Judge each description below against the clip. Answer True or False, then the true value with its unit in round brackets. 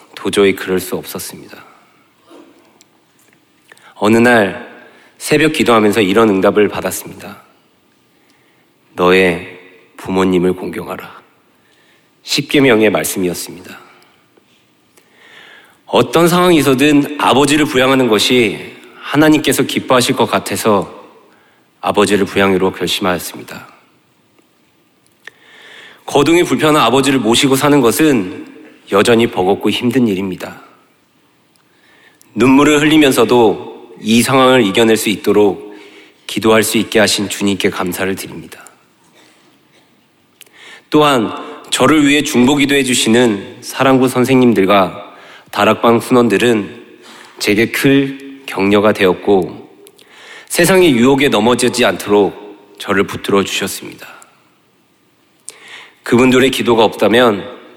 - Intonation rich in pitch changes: True (5.7 semitones)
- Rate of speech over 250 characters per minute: False (245 characters per minute)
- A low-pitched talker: True (120 Hz)